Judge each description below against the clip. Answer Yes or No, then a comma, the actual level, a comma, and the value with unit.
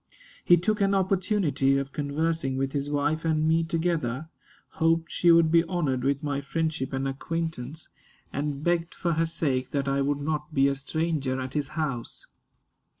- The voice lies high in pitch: No, medium, 155 Hz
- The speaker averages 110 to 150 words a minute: No, average, 170 wpm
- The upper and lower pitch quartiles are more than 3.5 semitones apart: No, average, 3.1 semitones